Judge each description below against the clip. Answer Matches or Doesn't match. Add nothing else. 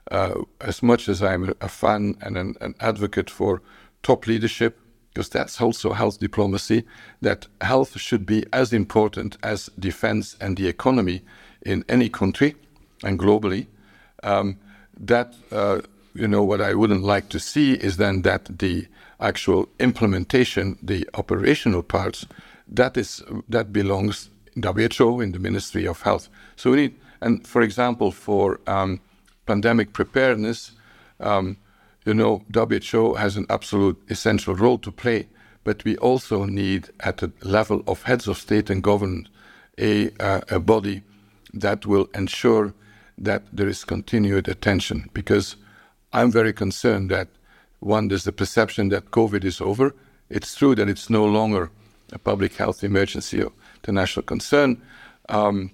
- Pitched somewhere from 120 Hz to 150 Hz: Doesn't match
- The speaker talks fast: Doesn't match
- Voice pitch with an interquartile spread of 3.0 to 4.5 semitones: Doesn't match